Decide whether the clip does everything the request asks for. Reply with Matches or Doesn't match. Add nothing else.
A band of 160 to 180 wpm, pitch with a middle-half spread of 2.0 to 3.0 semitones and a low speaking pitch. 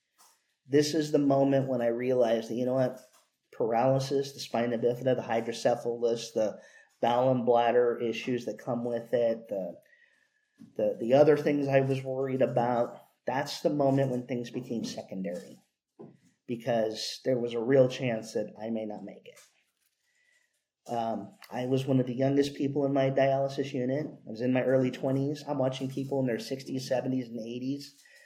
Matches